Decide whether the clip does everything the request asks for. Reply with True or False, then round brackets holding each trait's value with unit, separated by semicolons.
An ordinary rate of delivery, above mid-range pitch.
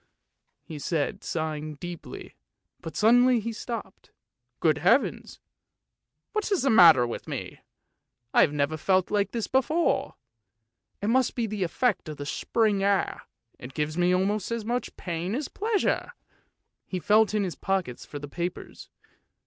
True (160 wpm; 195 Hz)